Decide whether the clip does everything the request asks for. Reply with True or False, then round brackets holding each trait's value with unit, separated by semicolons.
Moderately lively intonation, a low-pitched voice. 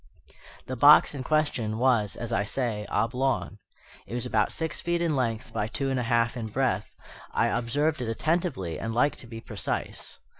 True (3.5 semitones; 120 Hz)